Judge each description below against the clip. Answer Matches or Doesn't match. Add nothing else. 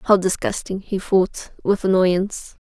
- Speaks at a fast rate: Doesn't match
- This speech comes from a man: Doesn't match